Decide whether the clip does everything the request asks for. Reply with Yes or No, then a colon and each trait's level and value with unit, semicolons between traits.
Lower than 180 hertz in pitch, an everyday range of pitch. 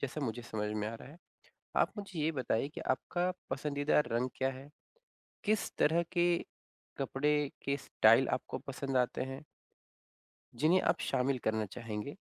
Yes: low, 135 Hz; average, 3.8 semitones